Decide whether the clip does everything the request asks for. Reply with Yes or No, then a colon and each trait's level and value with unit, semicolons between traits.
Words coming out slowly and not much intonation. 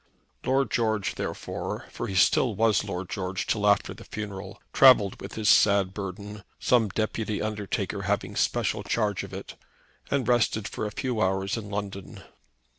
No: average, 160 wpm; narrow, 2.3 semitones